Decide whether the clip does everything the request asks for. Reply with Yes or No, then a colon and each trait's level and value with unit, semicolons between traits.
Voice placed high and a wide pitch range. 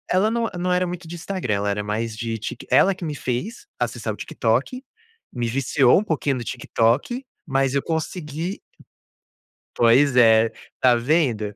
No: low, 135 Hz; wide, 7.4 semitones